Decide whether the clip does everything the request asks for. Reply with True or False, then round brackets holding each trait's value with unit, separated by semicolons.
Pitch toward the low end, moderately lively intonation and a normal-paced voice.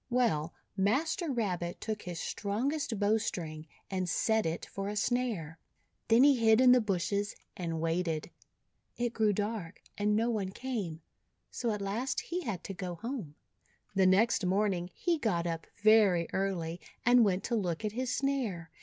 False (205 Hz; 4.9 semitones; 165 wpm)